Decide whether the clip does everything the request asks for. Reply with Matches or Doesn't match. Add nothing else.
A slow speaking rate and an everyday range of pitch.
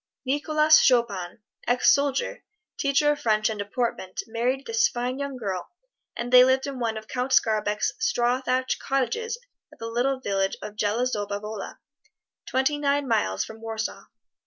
Doesn't match